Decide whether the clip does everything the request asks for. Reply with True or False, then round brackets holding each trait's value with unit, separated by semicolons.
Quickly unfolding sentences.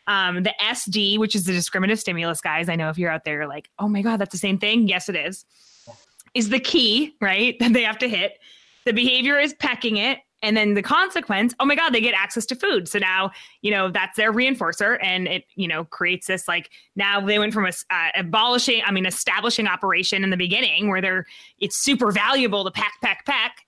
True (230 wpm)